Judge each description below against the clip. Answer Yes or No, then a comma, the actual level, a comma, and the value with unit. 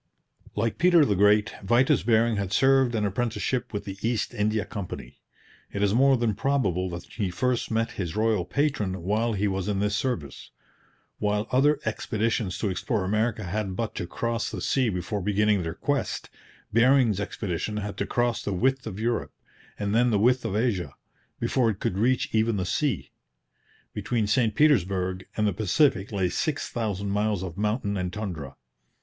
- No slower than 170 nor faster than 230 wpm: Yes, average, 175 wpm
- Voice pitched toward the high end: No, low, 105 Hz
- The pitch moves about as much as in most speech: Yes, average, 3.4 semitones